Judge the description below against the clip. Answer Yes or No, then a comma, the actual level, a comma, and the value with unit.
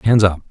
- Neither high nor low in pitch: No, low, 100 Hz